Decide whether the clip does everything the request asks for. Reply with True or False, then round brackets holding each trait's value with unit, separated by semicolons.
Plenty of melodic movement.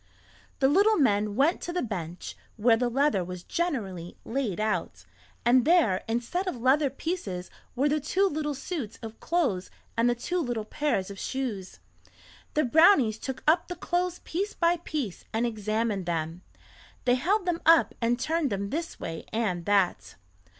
True (7.8 semitones)